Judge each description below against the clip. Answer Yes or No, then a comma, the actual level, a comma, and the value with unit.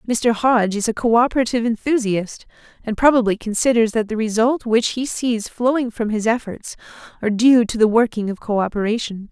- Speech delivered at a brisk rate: No, average, 165 wpm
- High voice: Yes, high, 225 Hz